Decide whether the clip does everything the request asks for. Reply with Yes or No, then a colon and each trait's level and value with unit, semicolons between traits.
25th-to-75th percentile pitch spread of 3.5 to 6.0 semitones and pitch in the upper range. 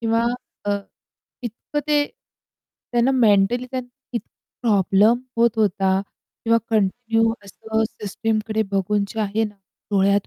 No: average, 2.7 semitones; high, 220 Hz